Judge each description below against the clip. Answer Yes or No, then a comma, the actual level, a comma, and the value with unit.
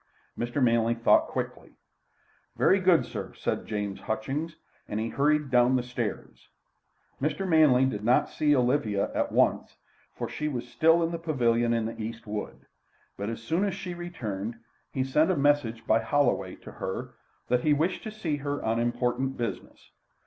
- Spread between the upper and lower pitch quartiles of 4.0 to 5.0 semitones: Yes, average, 4.7 semitones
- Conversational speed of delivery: Yes, average, 170 wpm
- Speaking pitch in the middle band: No, low, 125 Hz